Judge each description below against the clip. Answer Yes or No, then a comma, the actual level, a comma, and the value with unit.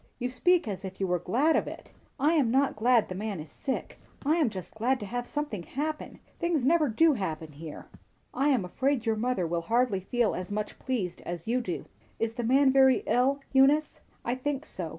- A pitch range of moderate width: No, wide, 6.1 semitones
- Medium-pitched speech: No, high, 245 Hz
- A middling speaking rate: No, fast, 210 wpm